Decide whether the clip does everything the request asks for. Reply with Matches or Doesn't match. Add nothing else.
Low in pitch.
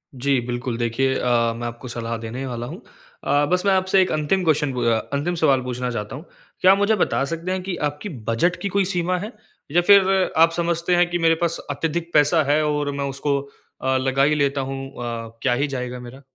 Doesn't match